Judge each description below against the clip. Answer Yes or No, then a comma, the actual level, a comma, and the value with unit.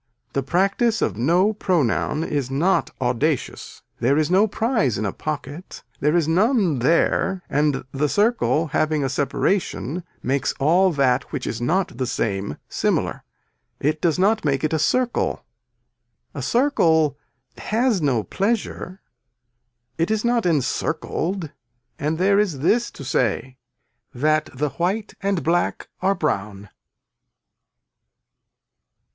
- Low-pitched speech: No, medium, 160 Hz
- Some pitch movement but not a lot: No, wide, 6.0 semitones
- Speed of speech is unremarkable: No, slow, 130 wpm